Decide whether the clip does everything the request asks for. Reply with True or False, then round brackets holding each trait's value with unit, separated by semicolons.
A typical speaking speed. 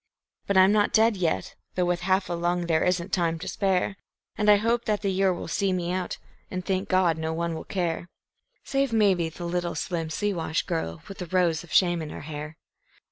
False (215 wpm)